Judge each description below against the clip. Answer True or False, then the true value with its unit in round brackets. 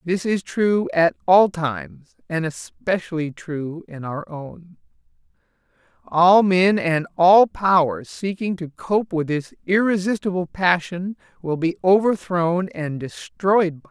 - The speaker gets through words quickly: False (135 wpm)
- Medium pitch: True (175 Hz)